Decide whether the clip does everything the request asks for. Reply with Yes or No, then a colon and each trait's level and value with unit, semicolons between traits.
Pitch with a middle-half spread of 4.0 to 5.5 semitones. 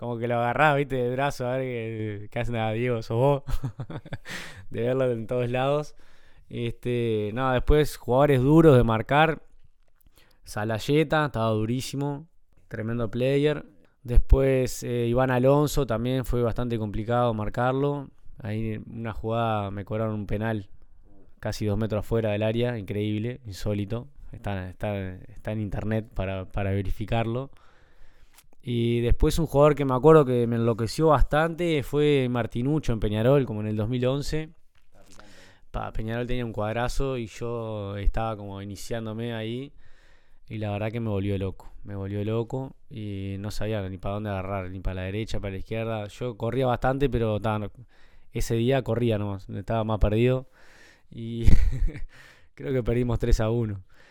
No: average, 3.3 semitones